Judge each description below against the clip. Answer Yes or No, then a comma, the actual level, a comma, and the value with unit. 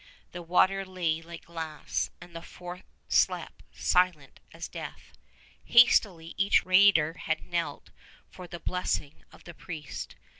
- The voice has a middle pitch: Yes, medium, 175 Hz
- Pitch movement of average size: No, narrow, 2.1 semitones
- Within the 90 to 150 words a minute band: Yes, slow, 135 wpm